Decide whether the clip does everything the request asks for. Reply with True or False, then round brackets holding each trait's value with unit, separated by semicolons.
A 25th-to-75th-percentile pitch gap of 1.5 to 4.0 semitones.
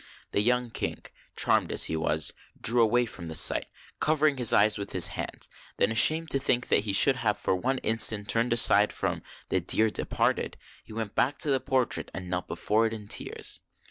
True (3.4 semitones)